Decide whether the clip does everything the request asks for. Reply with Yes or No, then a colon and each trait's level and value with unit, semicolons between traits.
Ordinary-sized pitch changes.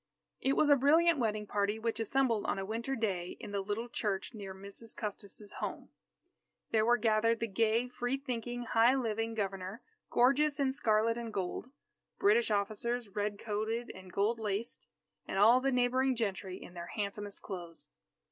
Yes: average, 3.2 semitones